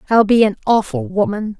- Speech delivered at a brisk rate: No, average, 190 wpm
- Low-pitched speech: No, high, 215 Hz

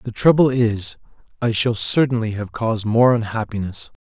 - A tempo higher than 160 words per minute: No, average, 145 wpm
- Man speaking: Yes, male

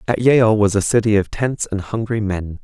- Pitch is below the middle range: Yes, low, 105 Hz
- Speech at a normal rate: No, fast, 230 wpm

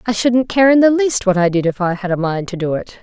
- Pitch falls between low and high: No, high, 210 Hz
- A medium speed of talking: No, fast, 335 wpm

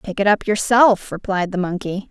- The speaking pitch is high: Yes, high, 195 Hz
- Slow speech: No, average, 200 wpm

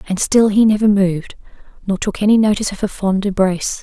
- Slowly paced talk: No, fast, 205 wpm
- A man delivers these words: No, female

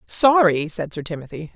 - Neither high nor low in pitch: Yes, medium, 175 Hz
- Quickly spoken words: No, average, 155 wpm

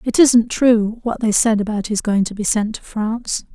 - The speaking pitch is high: Yes, high, 220 Hz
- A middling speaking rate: No, fast, 235 wpm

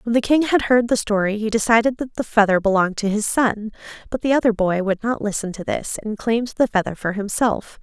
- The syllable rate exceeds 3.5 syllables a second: Yes, 5.8 syllables/s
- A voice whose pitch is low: No, high, 220 Hz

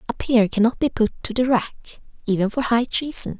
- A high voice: Yes, high, 235 Hz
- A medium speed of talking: No, fast, 210 wpm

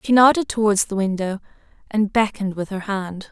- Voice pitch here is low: No, high, 205 Hz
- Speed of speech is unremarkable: Yes, average, 180 wpm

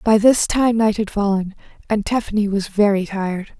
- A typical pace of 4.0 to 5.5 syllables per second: Yes, 5.2 syllables/s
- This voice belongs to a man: No, female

